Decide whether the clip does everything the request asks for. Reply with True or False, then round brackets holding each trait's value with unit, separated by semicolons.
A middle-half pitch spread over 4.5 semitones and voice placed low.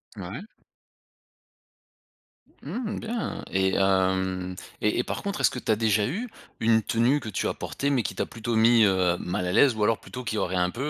True (5.0 semitones; 110 Hz)